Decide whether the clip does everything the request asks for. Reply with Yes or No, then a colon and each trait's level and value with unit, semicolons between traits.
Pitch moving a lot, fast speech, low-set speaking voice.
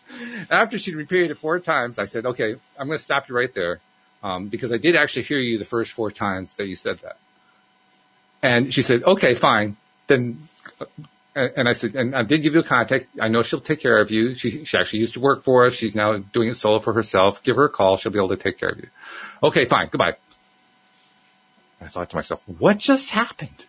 Yes: wide, 6.0 semitones; fast, 235 wpm; low, 125 Hz